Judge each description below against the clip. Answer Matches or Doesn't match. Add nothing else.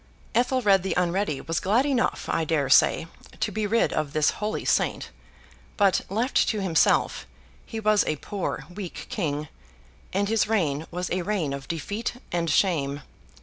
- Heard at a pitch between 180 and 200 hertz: Matches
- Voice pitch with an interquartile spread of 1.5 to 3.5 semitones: Doesn't match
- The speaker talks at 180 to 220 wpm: Doesn't match